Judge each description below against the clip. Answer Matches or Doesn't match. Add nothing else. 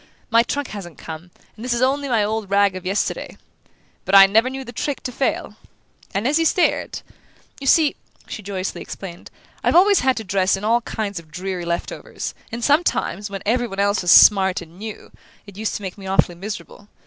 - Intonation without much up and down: Doesn't match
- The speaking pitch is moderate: Doesn't match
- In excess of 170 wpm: Matches